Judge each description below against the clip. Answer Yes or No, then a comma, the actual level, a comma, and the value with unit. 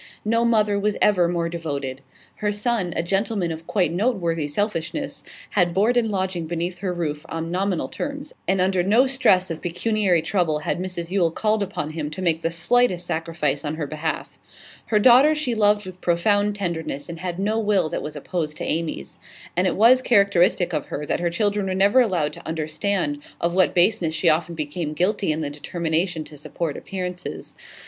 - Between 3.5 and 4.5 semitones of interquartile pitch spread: Yes, average, 4.0 semitones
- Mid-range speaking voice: Yes, medium, 180 Hz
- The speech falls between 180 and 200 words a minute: Yes, average, 190 wpm